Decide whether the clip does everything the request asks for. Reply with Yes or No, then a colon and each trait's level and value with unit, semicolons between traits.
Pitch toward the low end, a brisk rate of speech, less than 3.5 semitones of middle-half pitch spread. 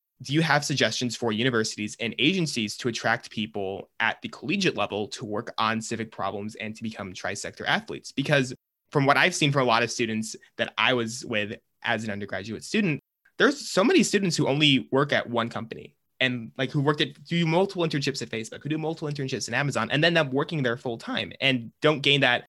No: low, 125 Hz; fast, 215 wpm; average, 4.9 semitones